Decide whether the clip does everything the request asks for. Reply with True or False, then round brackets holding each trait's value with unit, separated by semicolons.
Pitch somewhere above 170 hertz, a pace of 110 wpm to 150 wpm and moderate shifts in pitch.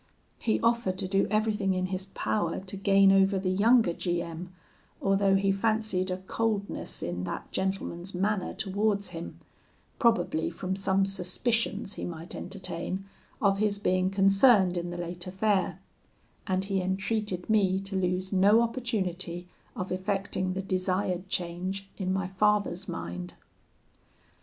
False (190 Hz; 140 wpm; 1.7 semitones)